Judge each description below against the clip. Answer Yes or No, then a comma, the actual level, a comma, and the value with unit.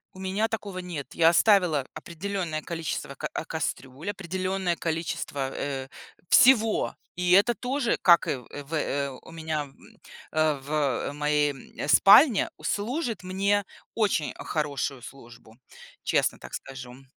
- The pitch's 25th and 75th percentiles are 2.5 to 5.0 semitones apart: No, wide, 5.5 semitones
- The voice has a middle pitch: Yes, medium, 165 Hz